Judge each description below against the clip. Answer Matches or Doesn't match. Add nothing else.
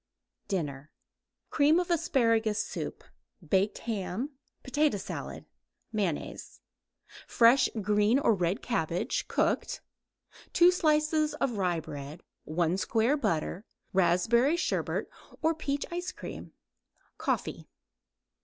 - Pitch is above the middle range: Matches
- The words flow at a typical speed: Doesn't match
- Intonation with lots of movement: Matches